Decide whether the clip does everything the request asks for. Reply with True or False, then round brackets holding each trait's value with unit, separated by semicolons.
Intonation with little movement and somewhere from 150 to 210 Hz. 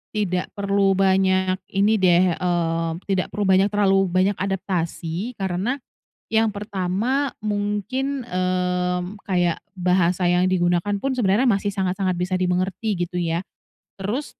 True (2.2 semitones; 190 Hz)